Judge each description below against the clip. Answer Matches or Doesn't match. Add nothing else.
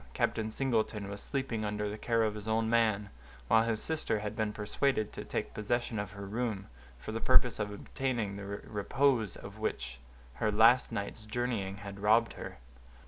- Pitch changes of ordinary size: Doesn't match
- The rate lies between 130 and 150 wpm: Doesn't match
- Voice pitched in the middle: Doesn't match